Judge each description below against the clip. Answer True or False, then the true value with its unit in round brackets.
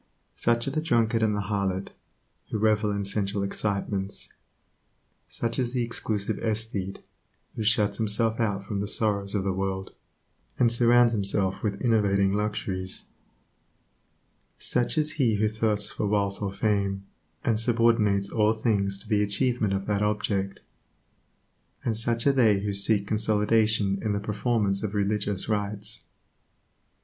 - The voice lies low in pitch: True (105 Hz)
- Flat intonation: True (2.2 semitones)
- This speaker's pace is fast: False (145 wpm)